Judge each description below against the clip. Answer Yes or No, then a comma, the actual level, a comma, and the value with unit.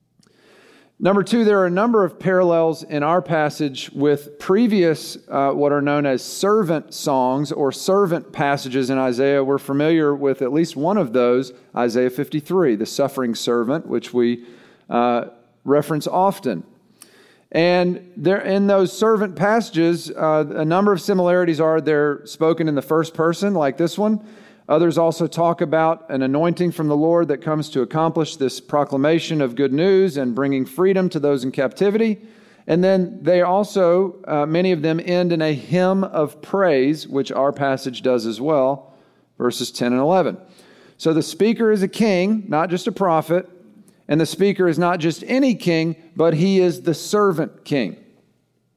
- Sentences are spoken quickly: No, average, 170 wpm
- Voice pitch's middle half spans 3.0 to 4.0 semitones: No, average, 4.9 semitones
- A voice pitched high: No, medium, 160 Hz